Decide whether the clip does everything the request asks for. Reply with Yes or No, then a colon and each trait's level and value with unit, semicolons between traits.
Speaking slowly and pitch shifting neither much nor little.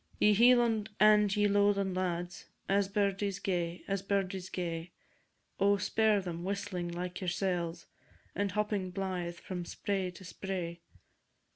No: slow, 130 wpm; narrow, 2.3 semitones